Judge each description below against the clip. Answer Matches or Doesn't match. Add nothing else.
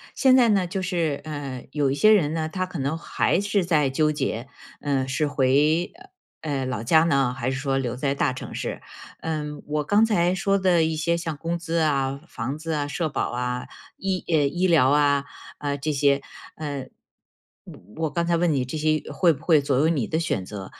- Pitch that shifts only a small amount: Doesn't match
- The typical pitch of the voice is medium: Matches